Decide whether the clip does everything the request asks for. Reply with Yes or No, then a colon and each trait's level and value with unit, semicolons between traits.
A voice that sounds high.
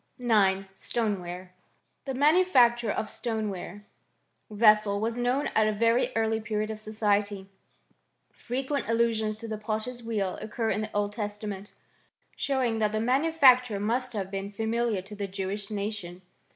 Yes: high, 215 Hz